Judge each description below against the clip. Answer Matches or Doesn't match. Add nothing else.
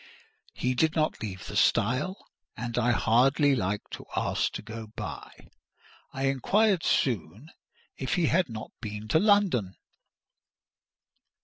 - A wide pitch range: Matches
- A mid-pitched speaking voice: Doesn't match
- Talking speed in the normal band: Doesn't match